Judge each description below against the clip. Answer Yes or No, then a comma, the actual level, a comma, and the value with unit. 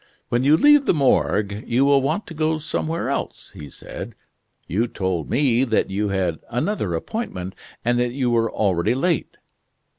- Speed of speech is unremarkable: Yes, average, 170 wpm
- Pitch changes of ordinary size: No, wide, 7.1 semitones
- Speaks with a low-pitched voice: Yes, low, 120 Hz